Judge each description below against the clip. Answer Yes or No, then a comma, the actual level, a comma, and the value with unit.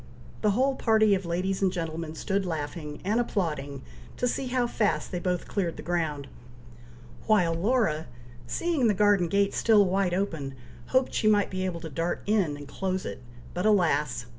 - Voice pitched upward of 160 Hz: Yes, medium, 185 Hz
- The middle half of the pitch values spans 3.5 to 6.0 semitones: Yes, average, 4.3 semitones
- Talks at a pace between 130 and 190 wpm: Yes, average, 175 wpm